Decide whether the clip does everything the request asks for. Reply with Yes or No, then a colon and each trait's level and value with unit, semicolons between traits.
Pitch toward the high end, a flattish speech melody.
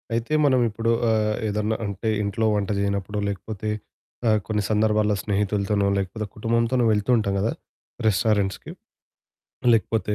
No: low, 105 Hz; narrow, 1.8 semitones